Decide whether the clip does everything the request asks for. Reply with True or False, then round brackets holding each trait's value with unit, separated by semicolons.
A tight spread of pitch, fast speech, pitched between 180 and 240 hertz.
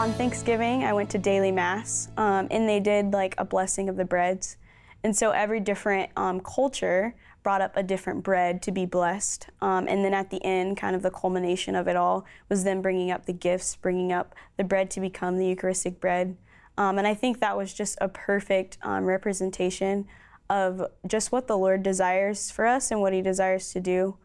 True (1.6 semitones; 210 wpm; 190 Hz)